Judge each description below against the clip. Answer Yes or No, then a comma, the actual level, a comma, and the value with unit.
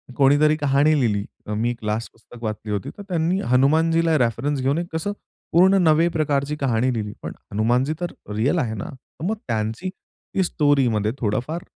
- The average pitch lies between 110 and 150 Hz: Yes, low, 135 Hz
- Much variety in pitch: Yes, wide, 5.9 semitones